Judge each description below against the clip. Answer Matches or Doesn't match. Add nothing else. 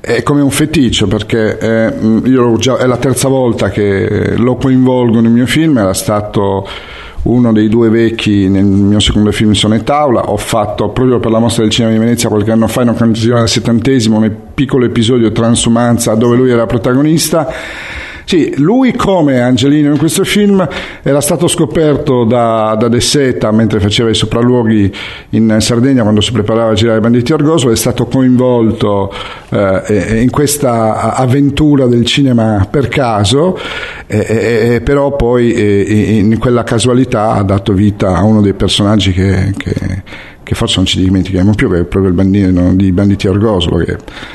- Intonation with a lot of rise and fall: Doesn't match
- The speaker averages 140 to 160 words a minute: Doesn't match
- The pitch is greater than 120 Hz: Doesn't match